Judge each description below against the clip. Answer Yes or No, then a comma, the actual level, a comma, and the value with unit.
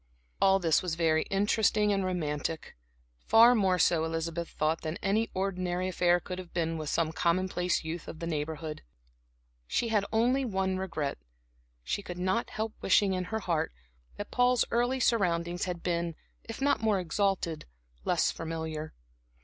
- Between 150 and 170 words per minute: Yes, average, 155 wpm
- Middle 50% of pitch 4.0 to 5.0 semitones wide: No, average, 3.6 semitones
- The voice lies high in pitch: No, medium, 180 Hz